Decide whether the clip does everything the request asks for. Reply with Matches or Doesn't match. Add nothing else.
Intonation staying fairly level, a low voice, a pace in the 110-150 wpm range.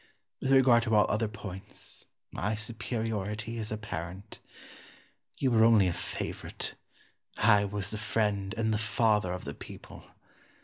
Matches